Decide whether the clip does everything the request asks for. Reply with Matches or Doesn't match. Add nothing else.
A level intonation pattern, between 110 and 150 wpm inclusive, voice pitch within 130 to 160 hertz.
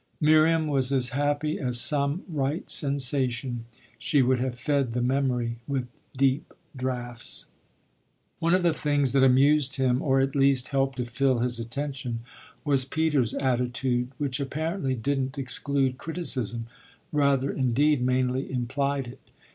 Matches